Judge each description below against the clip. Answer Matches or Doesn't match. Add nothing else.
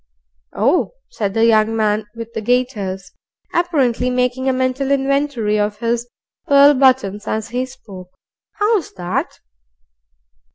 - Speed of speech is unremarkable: Doesn't match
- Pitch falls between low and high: Doesn't match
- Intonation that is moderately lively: Matches